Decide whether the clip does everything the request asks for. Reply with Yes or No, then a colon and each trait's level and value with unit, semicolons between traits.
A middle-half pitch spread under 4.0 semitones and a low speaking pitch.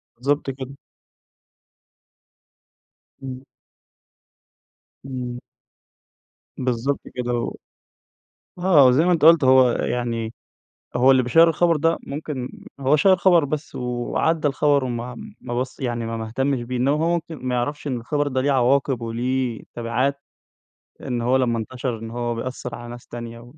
Yes: average, 2.9 semitones; low, 130 Hz